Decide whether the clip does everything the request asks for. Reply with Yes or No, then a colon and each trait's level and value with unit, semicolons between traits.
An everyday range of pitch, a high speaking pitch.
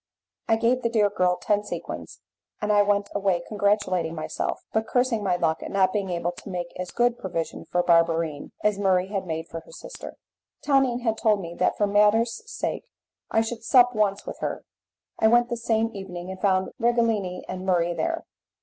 Yes: average, 3.8 semitones; high, 205 Hz